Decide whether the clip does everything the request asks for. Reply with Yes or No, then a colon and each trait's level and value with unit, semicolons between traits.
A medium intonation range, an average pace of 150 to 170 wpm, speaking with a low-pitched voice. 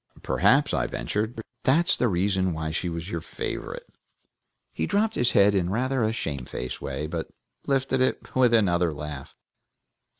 No: wide, 7.3 semitones; average, 155 wpm; low, 100 Hz